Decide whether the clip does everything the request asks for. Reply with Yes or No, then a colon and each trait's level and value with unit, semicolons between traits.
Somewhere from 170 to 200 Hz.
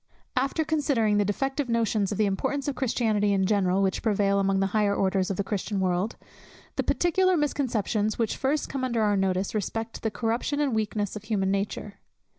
No: high, 215 Hz